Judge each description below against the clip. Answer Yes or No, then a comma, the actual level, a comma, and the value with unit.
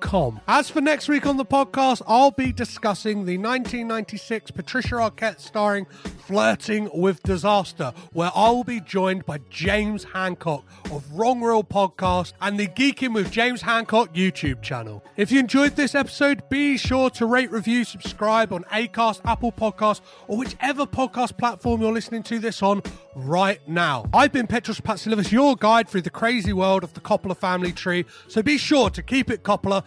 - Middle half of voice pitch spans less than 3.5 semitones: No, average, 4.4 semitones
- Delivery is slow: No, average, 175 wpm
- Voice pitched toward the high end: Yes, high, 215 Hz